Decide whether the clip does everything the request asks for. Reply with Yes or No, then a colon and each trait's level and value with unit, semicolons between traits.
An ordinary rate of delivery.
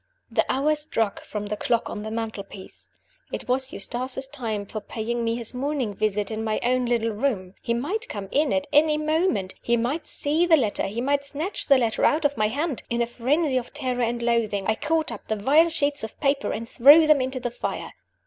No: fast, 215 wpm